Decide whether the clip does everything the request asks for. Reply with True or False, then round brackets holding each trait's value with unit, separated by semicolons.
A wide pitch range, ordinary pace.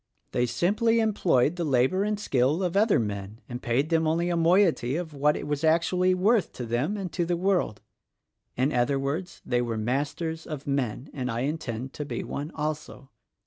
True (5.8 semitones; 190 wpm)